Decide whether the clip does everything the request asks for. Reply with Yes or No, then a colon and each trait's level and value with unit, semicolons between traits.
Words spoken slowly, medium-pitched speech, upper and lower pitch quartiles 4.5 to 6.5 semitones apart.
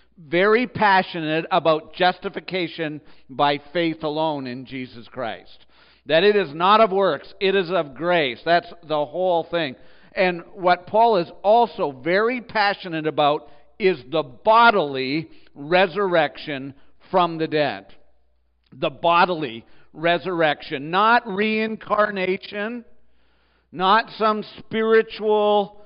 Yes: slow, 110 wpm; medium, 170 Hz; average, 5.2 semitones